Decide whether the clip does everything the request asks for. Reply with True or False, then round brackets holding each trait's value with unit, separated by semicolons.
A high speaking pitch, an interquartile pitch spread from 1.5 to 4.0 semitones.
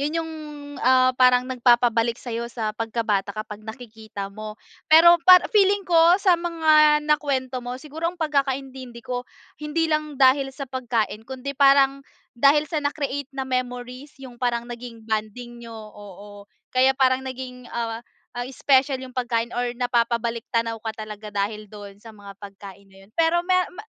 True (250 Hz; 3.7 semitones)